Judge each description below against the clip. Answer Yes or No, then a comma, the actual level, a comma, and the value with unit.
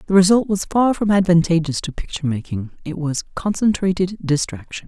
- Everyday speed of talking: Yes, average, 160 wpm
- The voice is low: No, medium, 175 Hz